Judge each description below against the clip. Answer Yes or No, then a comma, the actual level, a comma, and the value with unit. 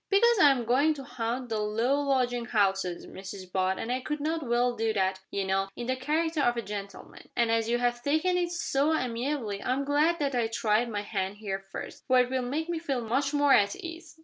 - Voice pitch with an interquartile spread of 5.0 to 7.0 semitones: Yes, average, 5.3 semitones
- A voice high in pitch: Yes, high, 245 Hz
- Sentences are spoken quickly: Yes, fast, 225 wpm